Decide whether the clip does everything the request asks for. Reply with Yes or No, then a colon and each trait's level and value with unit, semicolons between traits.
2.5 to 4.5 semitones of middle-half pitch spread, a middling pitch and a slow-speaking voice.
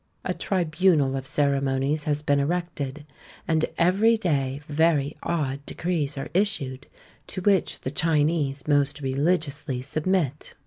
Yes: average, 3.4 semitones; medium, 150 Hz; slow, 125 wpm